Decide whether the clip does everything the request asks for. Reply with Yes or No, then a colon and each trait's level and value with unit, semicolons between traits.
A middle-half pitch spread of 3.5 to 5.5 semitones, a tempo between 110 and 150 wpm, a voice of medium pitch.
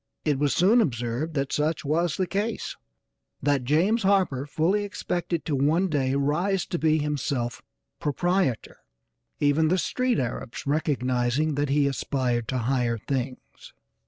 Yes: average, 4.8 semitones; average, 140 wpm; medium, 145 Hz